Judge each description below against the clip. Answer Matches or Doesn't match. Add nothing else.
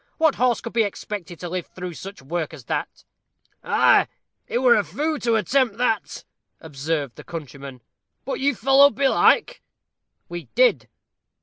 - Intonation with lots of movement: Matches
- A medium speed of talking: Matches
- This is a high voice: Matches